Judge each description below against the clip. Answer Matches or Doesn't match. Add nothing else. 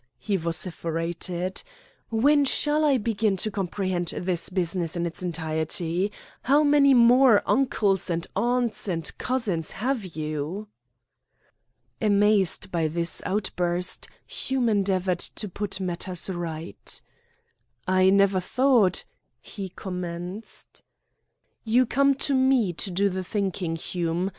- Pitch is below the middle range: Doesn't match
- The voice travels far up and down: Doesn't match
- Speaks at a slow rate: Matches